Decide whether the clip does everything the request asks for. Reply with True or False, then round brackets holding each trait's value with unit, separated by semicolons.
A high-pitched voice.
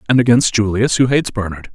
False (115 Hz)